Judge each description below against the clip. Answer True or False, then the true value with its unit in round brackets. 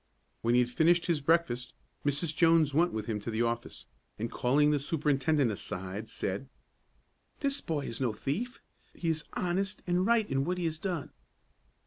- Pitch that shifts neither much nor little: False (6.0 semitones)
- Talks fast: False (175 wpm)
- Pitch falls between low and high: True (150 Hz)